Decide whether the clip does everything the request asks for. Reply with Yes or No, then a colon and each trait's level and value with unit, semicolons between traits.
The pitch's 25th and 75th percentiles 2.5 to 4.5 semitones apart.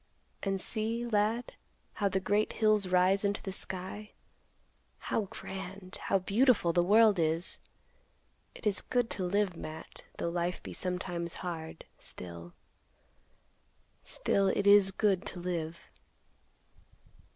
Yes: average, 2.8 semitones